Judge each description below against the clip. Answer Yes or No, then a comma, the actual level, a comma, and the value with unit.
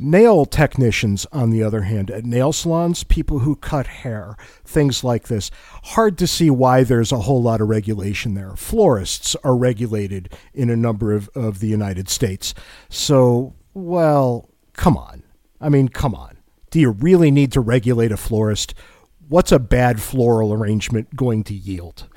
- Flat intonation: No, average, 5.0 semitones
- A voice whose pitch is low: Yes, low, 120 Hz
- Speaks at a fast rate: No, average, 170 wpm